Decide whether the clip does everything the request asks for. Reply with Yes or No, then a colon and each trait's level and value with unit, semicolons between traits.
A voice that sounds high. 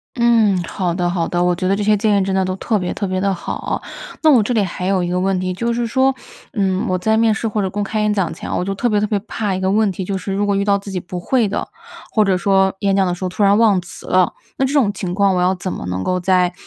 Yes: high, 195 Hz